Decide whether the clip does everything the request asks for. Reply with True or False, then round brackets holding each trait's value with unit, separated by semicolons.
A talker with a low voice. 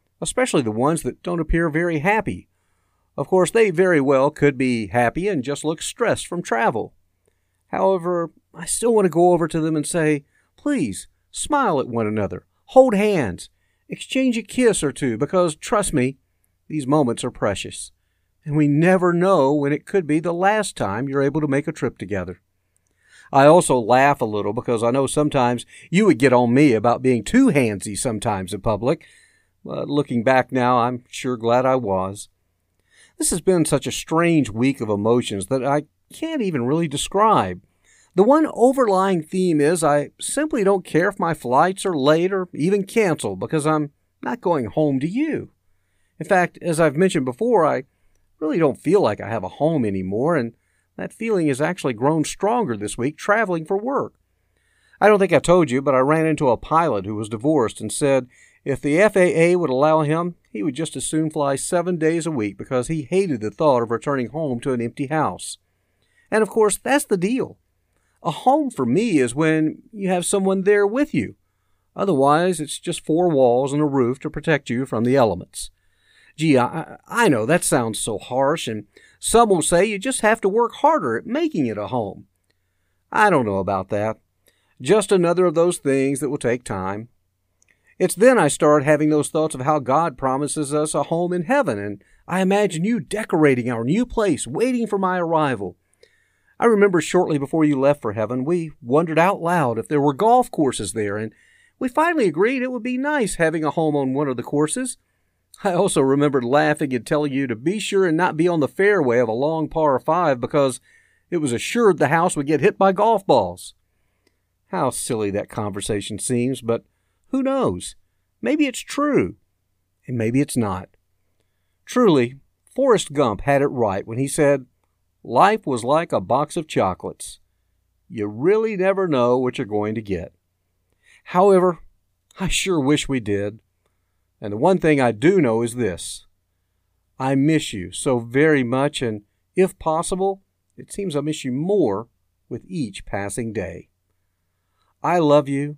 False (145 Hz)